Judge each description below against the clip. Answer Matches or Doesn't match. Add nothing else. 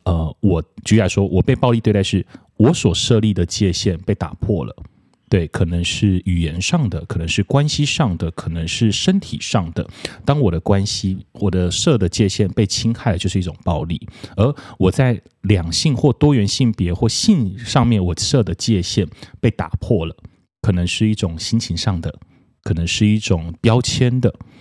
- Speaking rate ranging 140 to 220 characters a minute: Doesn't match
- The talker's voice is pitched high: Doesn't match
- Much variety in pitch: Doesn't match